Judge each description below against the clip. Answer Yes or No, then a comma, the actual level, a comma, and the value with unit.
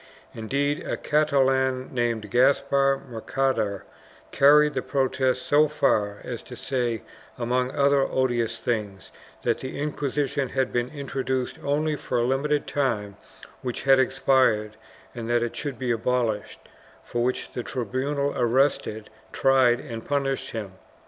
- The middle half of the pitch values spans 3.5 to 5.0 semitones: No, average, 2.7 semitones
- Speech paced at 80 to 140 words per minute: Yes, slow, 135 wpm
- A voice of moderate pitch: No, low, 130 Hz